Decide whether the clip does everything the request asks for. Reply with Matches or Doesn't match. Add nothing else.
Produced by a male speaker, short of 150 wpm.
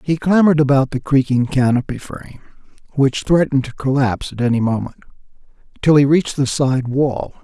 Doesn't match